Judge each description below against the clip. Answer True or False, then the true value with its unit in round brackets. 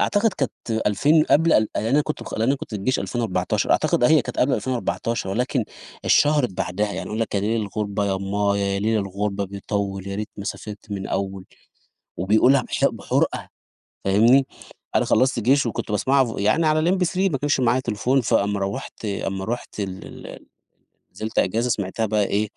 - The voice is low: True (110 Hz)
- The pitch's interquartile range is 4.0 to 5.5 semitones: True (4.6 semitones)